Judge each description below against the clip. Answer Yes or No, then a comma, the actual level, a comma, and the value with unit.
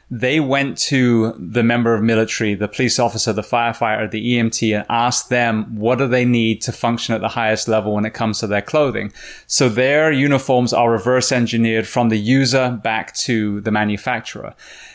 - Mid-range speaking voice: No, low, 115 Hz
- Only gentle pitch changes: Yes, narrow, 2.2 semitones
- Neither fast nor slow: Yes, average, 185 wpm